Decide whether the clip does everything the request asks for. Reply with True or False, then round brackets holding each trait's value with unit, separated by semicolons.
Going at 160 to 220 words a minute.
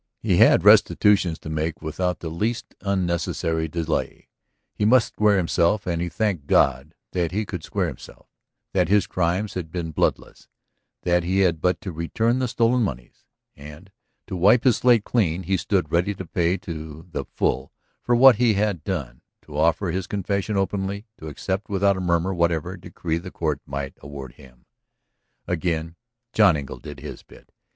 True (175 wpm)